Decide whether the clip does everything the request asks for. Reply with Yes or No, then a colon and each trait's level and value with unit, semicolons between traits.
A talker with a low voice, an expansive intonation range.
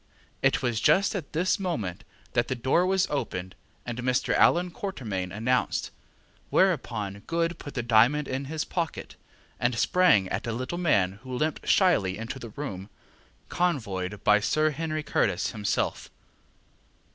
Yes: low, 130 Hz; wide, 7.5 semitones